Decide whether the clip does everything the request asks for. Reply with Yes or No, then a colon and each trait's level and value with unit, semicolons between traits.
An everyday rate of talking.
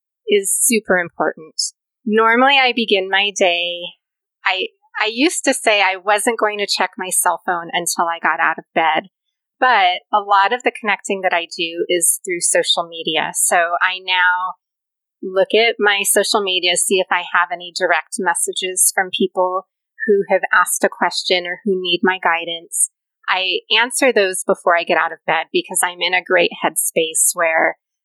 Yes: average, 180 wpm